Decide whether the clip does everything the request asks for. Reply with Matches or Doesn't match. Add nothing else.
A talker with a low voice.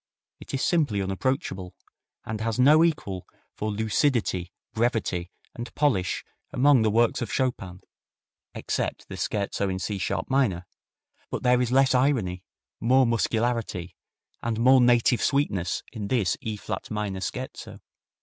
Matches